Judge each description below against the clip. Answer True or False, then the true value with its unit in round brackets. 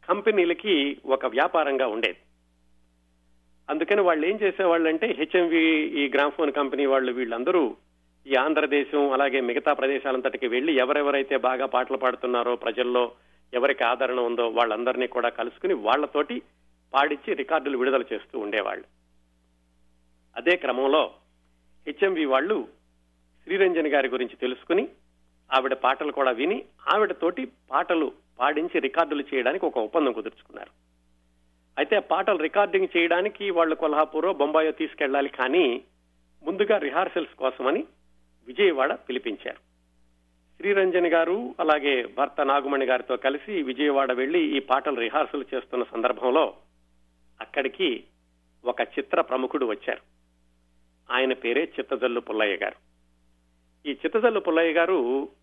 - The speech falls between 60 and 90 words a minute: False (110 wpm)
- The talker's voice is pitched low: True (130 Hz)